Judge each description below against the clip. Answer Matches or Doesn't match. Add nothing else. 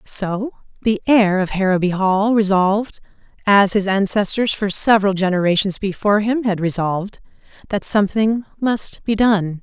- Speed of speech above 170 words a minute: Doesn't match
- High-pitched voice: Matches